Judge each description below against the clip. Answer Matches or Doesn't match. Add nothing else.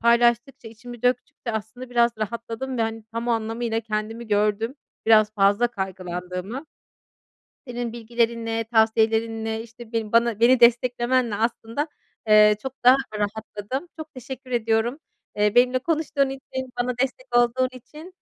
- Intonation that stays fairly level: Matches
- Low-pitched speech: Doesn't match